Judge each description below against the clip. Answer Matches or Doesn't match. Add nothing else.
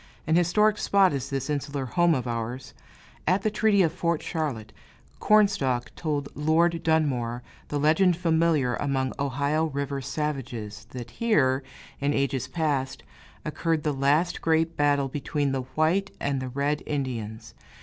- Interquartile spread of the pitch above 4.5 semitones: Doesn't match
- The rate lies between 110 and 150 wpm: Matches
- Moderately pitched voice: Matches